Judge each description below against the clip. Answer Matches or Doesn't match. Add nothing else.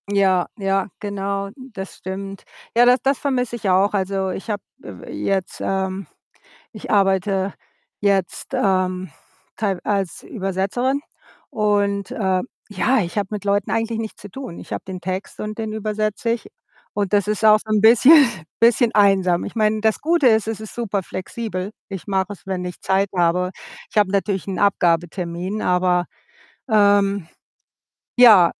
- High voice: Matches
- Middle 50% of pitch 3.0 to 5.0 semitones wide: Doesn't match